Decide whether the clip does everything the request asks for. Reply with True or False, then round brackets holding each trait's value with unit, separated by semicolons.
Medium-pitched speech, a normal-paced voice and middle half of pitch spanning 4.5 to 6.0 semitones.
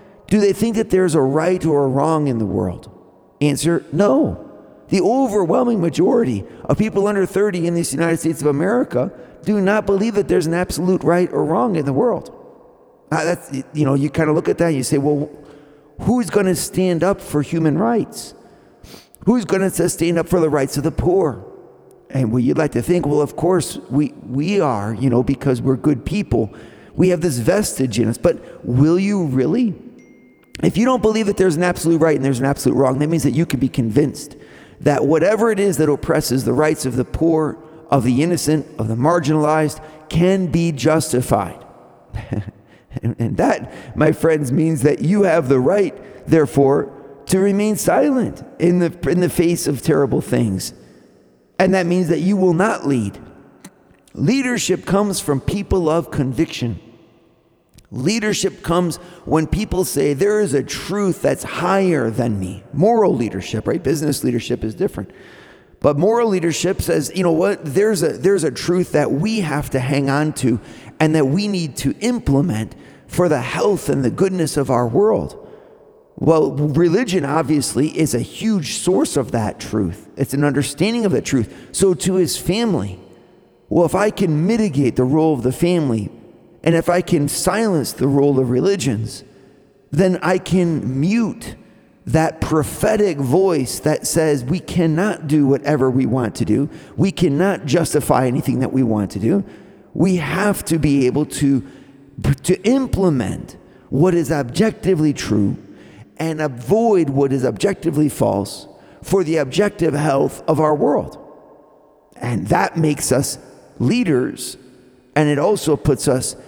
True (155 Hz; 170 wpm; 5.2 semitones)